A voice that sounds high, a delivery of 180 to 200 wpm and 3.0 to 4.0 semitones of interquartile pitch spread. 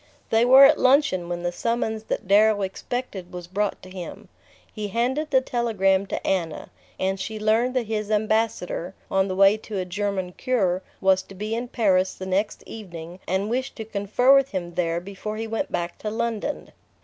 Yes: high, 205 Hz; average, 190 wpm; average, 3.5 semitones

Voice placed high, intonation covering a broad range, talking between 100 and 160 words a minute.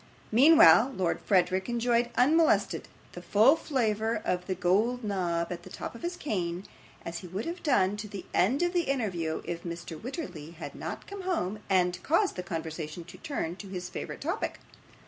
No: high, 200 Hz; wide, 7.0 semitones; average, 185 wpm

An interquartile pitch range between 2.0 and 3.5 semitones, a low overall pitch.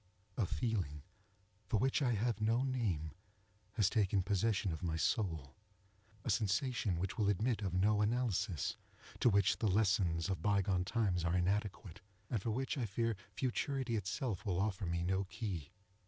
No: average, 3.9 semitones; low, 100 Hz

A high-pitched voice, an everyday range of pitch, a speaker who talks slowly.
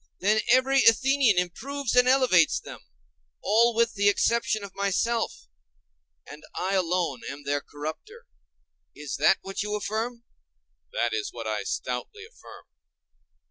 No: high, 200 Hz; wide, 8.2 semitones; slow, 130 wpm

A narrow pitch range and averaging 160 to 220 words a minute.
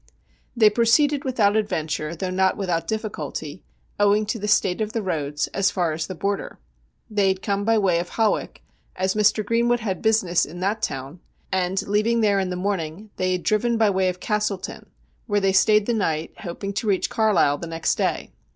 No: average, 3.2 semitones; average, 195 wpm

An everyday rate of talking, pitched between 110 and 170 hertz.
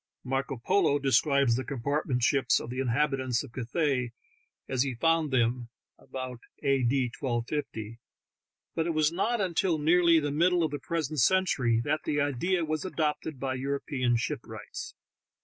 Yes: average, 150 wpm; medium, 140 Hz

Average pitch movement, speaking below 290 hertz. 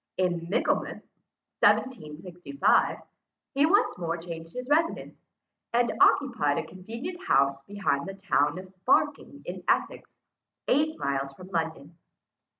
No: wide, 7.5 semitones; medium, 185 Hz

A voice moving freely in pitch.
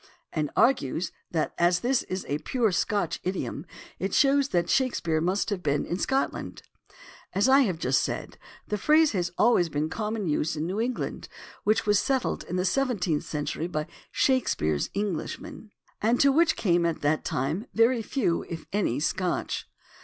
Yes: wide, 6.9 semitones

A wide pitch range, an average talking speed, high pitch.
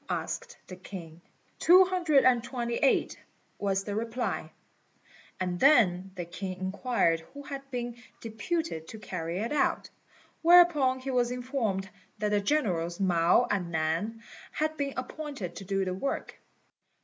Yes: wide, 6.8 semitones; average, 145 wpm; high, 225 Hz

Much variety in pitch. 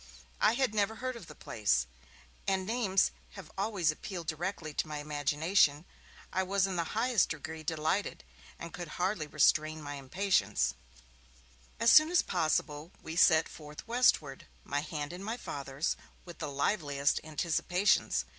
No: average, 4.8 semitones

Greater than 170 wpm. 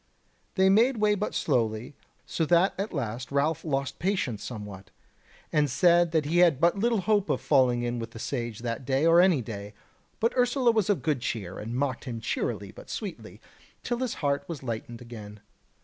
Yes: average, 190 wpm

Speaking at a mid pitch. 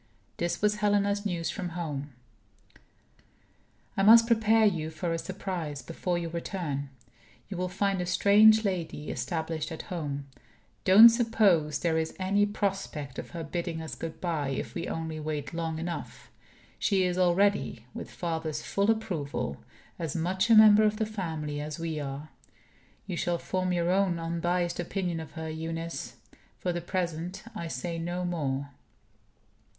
Yes: medium, 175 Hz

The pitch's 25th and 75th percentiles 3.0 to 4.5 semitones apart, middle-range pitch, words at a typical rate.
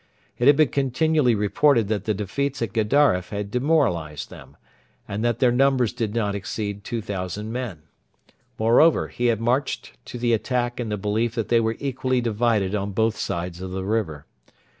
No: average, 3.5 semitones; low, 115 Hz; average, 175 wpm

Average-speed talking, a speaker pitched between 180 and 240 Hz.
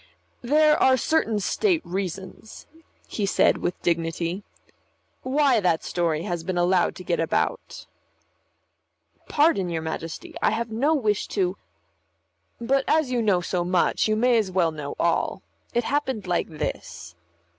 Yes: average, 145 wpm; high, 190 Hz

